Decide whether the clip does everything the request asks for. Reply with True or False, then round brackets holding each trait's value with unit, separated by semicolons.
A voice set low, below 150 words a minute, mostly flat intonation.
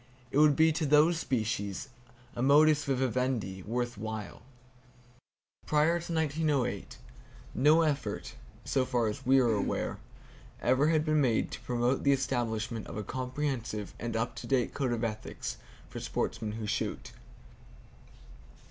False (130 Hz; 140 wpm; 4.7 semitones)